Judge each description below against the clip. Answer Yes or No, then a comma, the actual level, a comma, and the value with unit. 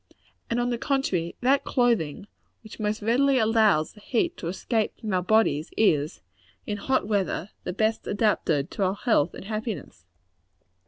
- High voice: Yes, high, 215 Hz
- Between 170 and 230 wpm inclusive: No, average, 160 wpm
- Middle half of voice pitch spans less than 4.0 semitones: No, average, 4.4 semitones